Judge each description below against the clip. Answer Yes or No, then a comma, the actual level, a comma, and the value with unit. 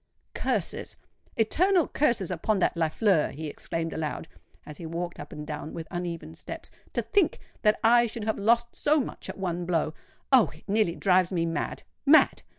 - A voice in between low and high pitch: Yes, medium, 180 Hz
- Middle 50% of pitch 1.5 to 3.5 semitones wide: No, wide, 5.5 semitones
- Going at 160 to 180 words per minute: Yes, average, 165 wpm